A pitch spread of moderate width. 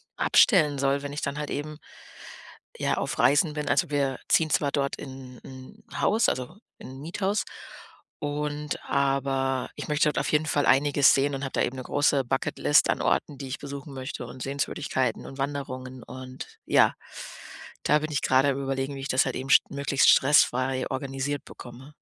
No: narrow, 1.7 semitones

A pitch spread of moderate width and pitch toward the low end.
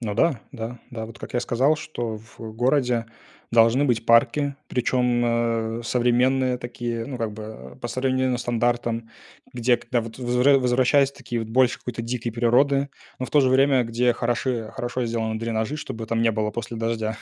No: narrow, 1.9 semitones; low, 120 Hz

